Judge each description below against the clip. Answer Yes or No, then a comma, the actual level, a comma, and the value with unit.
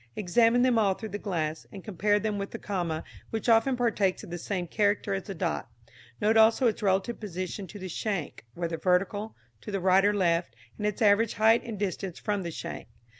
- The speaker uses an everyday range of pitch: Yes, average, 3.0 semitones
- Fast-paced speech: Yes, fast, 210 wpm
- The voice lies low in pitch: No, high, 200 Hz